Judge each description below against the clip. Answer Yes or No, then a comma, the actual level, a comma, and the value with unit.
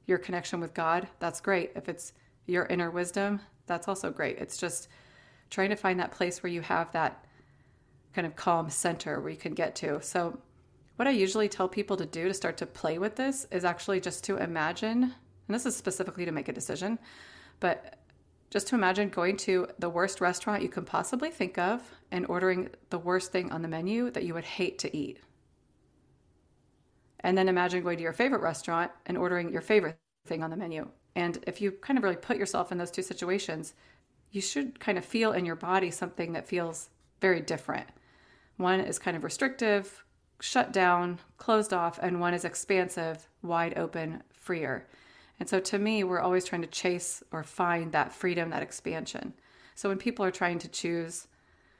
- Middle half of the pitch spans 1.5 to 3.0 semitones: Yes, average, 2.7 semitones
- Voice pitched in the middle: Yes, medium, 180 Hz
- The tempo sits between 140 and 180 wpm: No, average, 195 wpm